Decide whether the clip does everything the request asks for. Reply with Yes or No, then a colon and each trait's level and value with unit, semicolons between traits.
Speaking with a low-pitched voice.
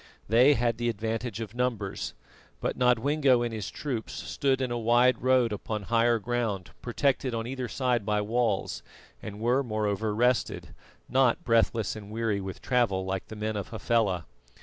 Yes: low, 115 Hz